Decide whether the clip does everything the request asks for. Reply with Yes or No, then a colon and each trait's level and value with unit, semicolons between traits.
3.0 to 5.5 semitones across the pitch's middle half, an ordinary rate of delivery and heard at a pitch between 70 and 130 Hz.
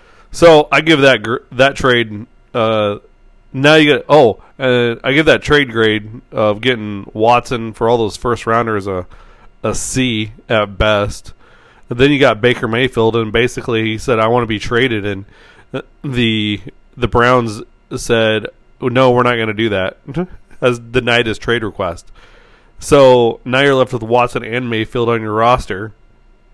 No: narrow, 2.6 semitones; average, 165 wpm; low, 120 Hz